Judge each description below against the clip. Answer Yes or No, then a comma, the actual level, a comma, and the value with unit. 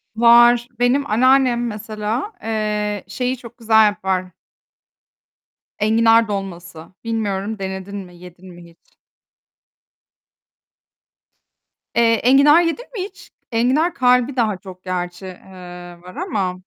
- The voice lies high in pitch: Yes, high, 215 Hz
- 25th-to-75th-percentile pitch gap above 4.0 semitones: Yes, average, 4.6 semitones